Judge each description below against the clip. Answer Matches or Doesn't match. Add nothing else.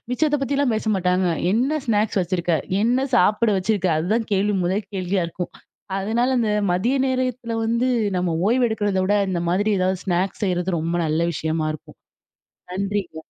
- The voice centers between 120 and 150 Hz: Doesn't match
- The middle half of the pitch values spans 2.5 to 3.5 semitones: Doesn't match